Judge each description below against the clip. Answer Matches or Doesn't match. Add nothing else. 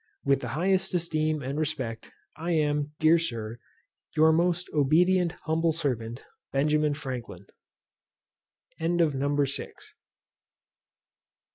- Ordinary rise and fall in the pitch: Matches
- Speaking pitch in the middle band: Matches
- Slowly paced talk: Matches